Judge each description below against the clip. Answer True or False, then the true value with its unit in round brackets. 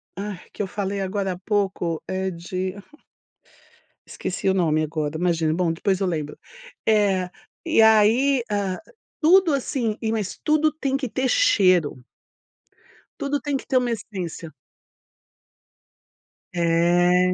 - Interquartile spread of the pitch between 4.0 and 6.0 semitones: True (4.6 semitones)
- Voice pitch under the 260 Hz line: True (190 Hz)